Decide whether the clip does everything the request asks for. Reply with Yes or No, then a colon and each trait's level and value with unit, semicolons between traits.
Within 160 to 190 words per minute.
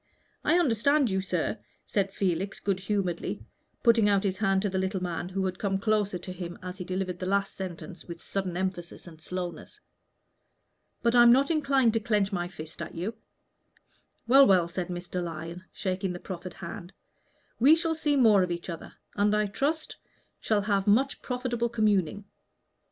Yes: average, 175 wpm